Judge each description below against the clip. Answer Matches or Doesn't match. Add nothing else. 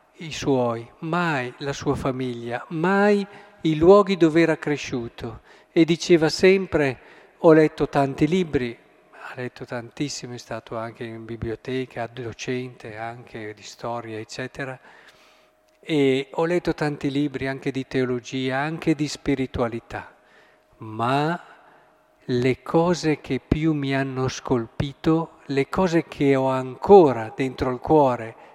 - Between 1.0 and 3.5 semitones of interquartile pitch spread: Doesn't match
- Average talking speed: Matches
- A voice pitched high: Doesn't match